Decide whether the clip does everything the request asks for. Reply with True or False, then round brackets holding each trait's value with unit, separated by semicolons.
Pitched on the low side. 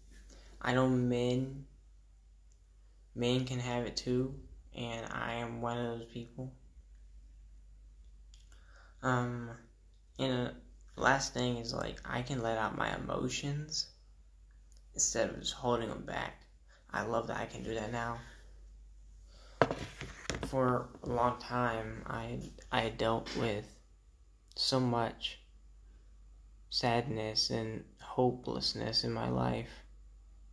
True (115 Hz)